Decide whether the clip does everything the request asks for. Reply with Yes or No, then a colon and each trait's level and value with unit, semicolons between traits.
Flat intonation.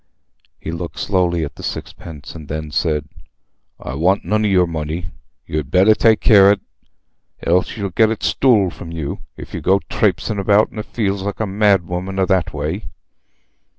No: average, 3.8 semitones